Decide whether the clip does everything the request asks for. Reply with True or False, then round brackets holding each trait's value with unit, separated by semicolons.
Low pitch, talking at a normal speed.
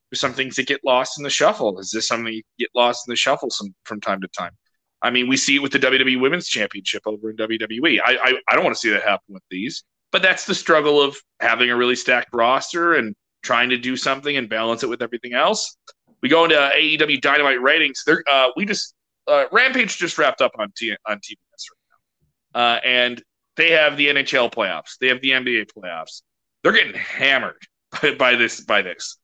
False (130 Hz; 220 wpm)